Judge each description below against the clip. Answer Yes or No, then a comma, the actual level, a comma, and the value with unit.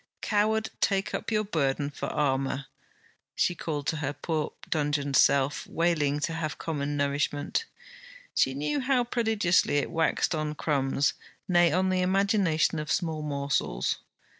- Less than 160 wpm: Yes, average, 140 wpm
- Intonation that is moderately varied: Yes, average, 4.2 semitones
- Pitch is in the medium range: Yes, medium, 155 Hz